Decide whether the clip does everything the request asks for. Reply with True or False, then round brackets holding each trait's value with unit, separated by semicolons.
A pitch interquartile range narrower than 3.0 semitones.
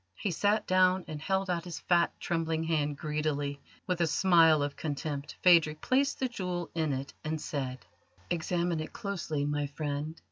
False (3.3 semitones)